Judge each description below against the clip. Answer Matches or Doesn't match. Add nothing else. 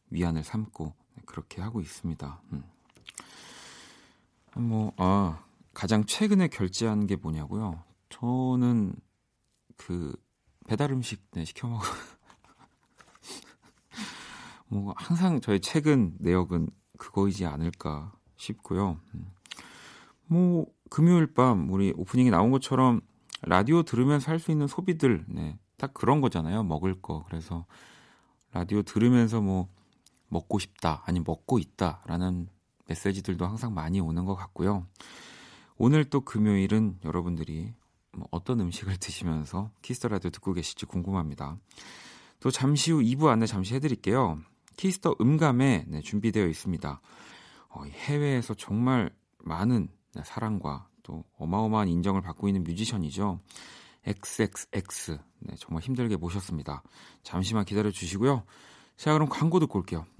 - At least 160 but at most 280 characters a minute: Matches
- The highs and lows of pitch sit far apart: Matches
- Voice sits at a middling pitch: Doesn't match